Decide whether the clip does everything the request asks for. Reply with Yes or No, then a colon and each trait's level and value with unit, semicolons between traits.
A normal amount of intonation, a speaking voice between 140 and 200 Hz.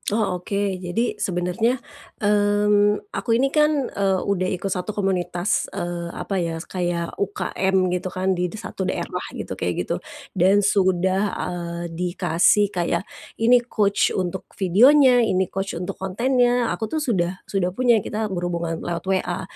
Yes: average, 3.0 semitones; high, 190 Hz